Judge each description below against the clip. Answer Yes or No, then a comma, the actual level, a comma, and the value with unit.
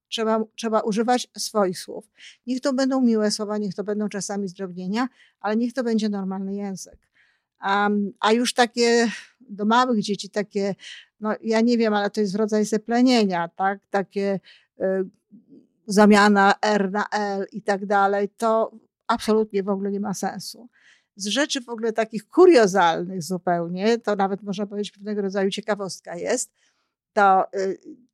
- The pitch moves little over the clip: Yes, narrow, 2.3 semitones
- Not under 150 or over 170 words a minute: Yes, average, 155 wpm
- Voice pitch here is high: Yes, high, 210 Hz